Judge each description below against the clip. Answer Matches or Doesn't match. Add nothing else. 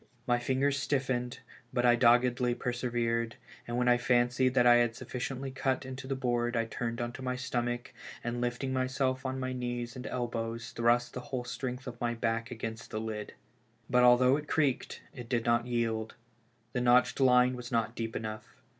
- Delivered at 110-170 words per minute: Doesn't match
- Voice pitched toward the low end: Matches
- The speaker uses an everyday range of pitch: Doesn't match